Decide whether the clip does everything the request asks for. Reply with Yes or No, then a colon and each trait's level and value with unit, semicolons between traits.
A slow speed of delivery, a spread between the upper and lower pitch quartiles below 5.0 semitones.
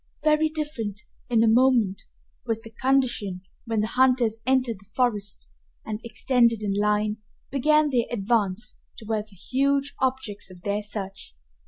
No: average, 145 wpm; average, 3.9 semitones